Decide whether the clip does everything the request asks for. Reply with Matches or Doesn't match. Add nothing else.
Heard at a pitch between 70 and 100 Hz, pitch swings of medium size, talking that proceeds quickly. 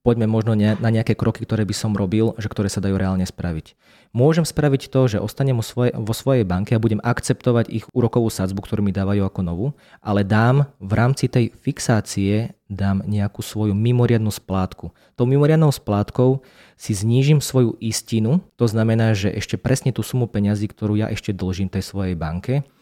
Doesn't match